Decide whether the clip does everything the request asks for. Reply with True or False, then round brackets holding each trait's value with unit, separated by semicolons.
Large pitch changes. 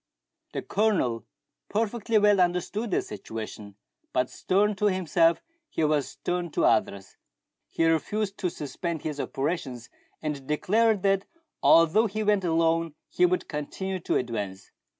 True (5.7 semitones)